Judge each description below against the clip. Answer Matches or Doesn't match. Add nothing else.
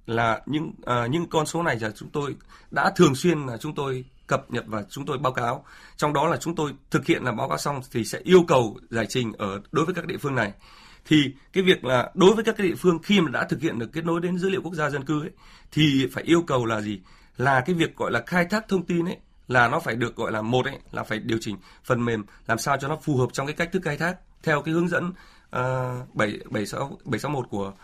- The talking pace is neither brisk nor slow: Doesn't match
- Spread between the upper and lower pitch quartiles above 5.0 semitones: Matches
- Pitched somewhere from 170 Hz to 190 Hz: Doesn't match